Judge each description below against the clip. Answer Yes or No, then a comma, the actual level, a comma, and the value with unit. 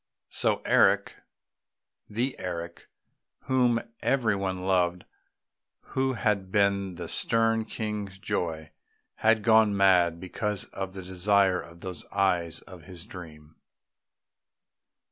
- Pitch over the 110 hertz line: No, very low, 95 Hz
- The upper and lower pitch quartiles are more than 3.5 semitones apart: No, average, 3.1 semitones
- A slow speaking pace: Yes, slow, 110 wpm